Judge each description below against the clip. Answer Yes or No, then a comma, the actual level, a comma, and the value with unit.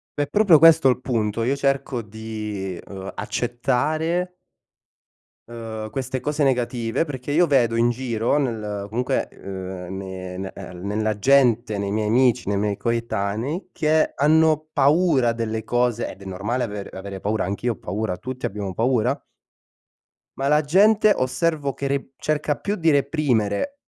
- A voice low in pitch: Yes, low, 120 Hz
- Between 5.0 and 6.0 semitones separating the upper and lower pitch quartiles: Yes, average, 5.3 semitones